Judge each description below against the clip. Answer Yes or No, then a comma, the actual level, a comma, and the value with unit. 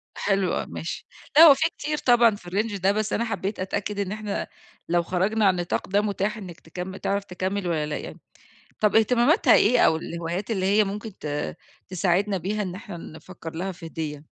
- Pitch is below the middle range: No, high, 195 Hz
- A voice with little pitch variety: No, average, 3.2 semitones